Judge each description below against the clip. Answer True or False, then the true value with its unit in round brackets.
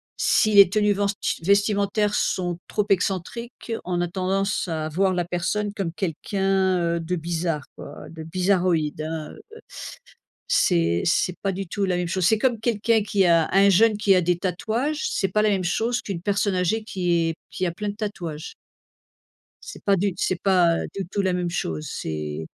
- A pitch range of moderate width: True (3.0 semitones)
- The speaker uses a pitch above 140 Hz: True (185 Hz)